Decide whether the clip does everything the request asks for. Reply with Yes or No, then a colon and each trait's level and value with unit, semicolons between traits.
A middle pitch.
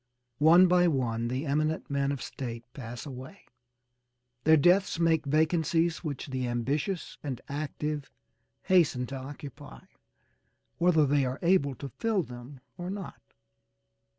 Yes: medium, 145 Hz